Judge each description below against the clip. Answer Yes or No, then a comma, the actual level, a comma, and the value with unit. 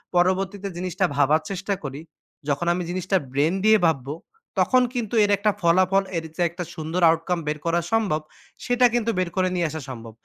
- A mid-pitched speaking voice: Yes, medium, 180 Hz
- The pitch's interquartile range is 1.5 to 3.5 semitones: No, average, 3.9 semitones